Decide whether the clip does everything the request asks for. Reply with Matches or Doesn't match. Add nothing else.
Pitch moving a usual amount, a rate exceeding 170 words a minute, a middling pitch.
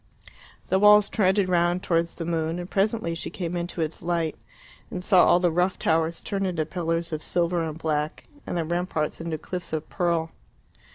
Doesn't match